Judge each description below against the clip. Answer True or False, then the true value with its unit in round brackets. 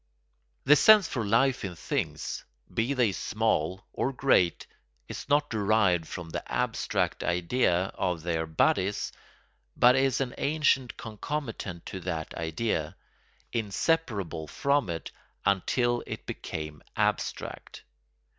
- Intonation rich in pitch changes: True (7.0 semitones)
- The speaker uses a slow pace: True (115 wpm)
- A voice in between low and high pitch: False (105 Hz)